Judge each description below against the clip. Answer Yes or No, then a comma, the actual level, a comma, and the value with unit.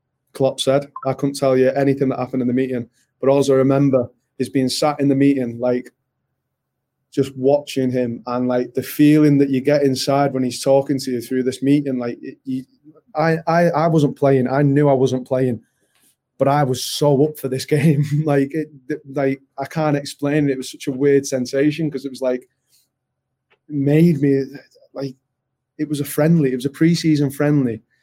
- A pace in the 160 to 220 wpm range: Yes, average, 195 wpm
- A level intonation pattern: Yes, narrow, 2.0 semitones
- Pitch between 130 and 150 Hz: Yes, medium, 140 Hz